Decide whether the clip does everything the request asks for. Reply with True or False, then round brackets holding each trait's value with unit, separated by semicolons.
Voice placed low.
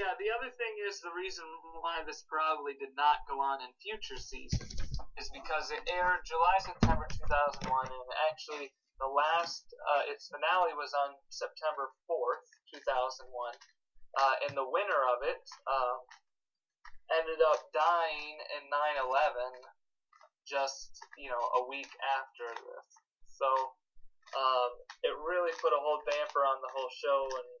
False (150 Hz)